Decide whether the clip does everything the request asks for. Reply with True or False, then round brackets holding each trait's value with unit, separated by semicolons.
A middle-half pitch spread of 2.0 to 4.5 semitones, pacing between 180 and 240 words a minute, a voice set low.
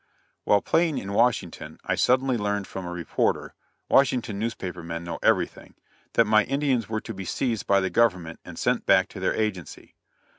True (4.0 semitones; 185 wpm; 105 Hz)